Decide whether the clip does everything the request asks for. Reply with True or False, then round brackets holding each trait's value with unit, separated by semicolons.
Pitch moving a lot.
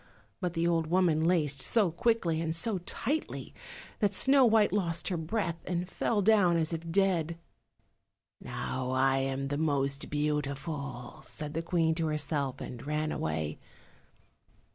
False (4.1 semitones)